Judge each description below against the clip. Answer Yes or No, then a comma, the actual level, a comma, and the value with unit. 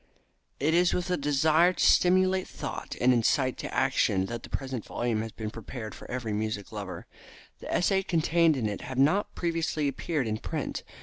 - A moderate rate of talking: Yes, average, 185 wpm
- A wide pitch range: Yes, wide, 7.0 semitones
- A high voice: No, low, 135 Hz